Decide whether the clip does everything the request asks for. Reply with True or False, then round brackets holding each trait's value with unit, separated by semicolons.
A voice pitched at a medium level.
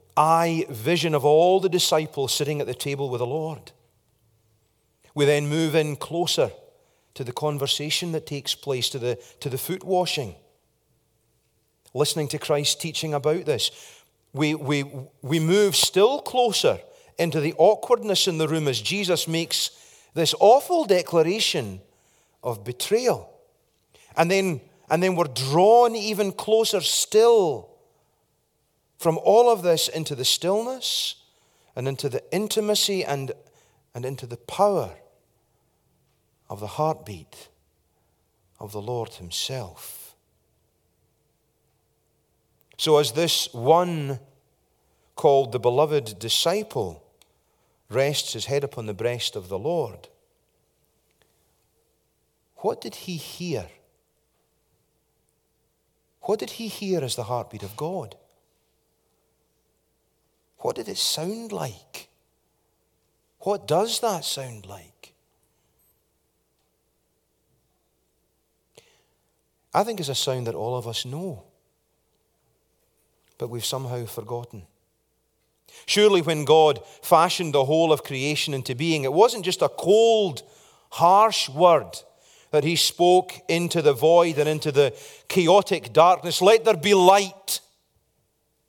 True (150 Hz)